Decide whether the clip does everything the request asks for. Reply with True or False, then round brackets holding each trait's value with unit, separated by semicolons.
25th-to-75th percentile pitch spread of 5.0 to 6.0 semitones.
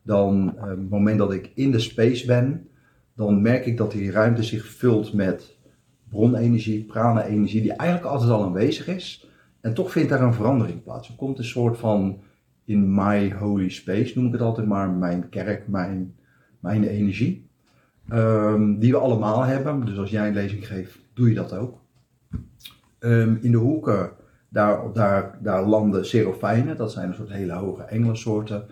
False (3.1 semitones)